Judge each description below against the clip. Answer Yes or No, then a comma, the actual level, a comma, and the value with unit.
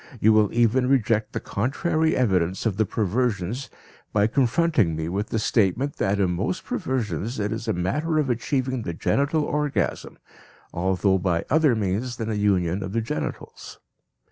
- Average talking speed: Yes, average, 165 wpm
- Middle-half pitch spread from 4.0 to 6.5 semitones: Yes, average, 5.2 semitones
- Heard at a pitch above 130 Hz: No, low, 110 Hz